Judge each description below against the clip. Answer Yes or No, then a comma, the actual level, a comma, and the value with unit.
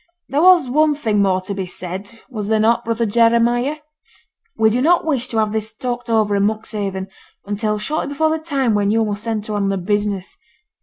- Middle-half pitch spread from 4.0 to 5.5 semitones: No, average, 3.2 semitones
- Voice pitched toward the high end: Yes, high, 220 Hz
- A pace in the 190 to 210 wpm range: Yes, average, 200 wpm